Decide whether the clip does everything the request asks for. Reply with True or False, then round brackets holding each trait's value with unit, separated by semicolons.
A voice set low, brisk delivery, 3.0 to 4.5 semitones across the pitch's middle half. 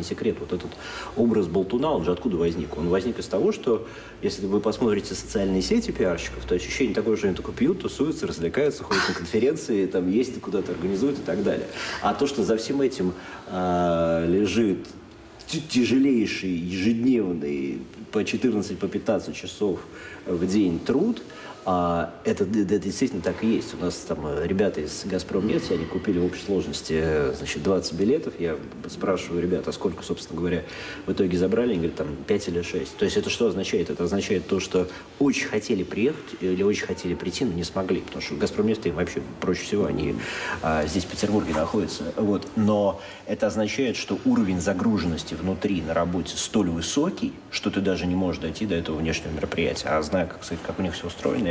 True (90 Hz; 180 wpm; 3.4 semitones)